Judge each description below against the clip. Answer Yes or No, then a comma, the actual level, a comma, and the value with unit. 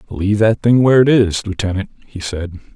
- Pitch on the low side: Yes, low, 100 Hz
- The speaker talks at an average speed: Yes, average, 195 wpm